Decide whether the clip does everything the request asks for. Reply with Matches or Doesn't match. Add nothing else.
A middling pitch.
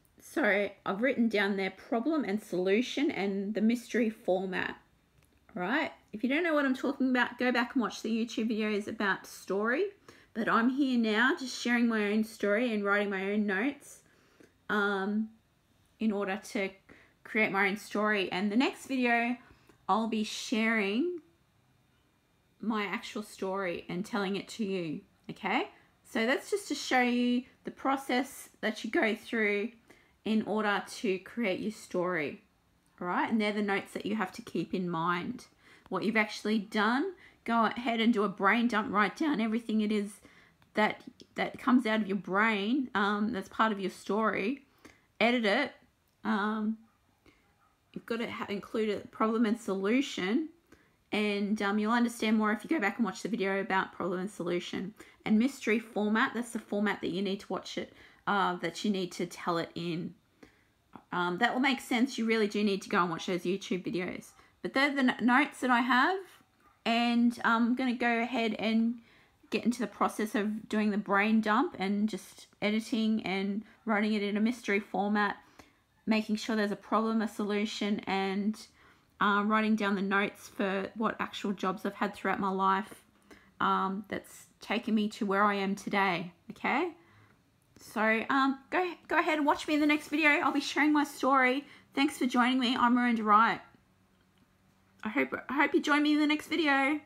Doesn't match